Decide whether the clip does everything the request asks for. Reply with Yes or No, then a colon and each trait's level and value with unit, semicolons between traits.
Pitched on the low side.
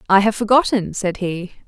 No: high, 205 Hz